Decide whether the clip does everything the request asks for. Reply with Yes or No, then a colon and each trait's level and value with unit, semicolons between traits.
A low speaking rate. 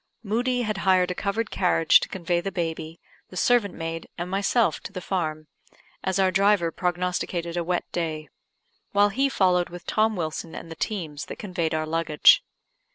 No: average, 175 wpm